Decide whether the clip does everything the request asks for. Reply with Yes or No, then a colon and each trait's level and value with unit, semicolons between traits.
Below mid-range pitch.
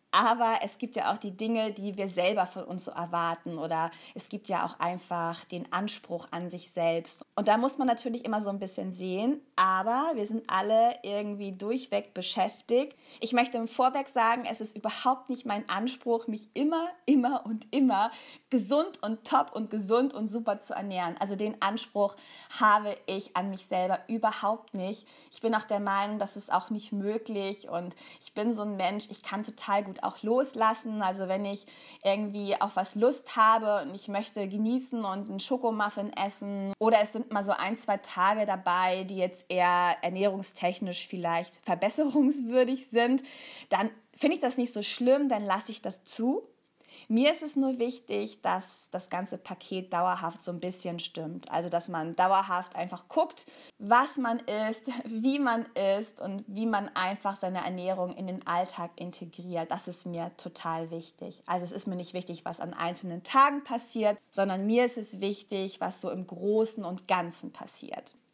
No: high, 205 Hz